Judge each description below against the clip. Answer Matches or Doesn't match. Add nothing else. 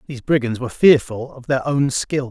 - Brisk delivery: Matches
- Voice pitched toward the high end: Doesn't match